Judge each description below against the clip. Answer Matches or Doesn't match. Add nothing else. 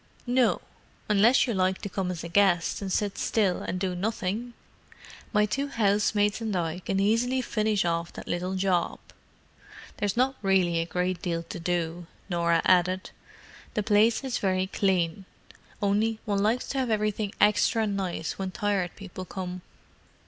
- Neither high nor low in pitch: Doesn't match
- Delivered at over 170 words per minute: Doesn't match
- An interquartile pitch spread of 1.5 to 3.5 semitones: Matches